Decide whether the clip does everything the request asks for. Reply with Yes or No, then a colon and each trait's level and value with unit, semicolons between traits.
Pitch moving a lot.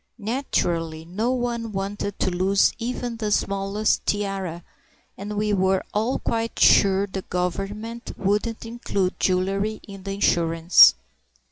No: narrow, 2.6 semitones